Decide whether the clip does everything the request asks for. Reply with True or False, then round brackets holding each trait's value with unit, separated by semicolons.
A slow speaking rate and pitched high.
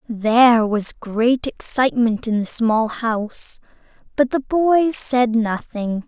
True (130 wpm; 235 Hz)